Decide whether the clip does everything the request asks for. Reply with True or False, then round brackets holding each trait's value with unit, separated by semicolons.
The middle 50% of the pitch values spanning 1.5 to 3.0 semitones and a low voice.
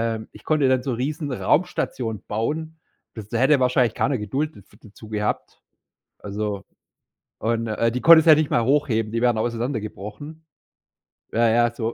False (4.8 semitones; 120 Hz)